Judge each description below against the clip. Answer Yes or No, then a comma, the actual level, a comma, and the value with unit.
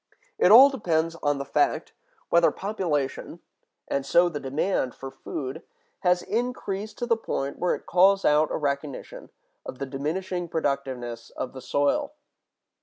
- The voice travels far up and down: Yes, wide, 5.7 semitones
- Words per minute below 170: Yes, average, 140 wpm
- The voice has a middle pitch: Yes, medium, 160 Hz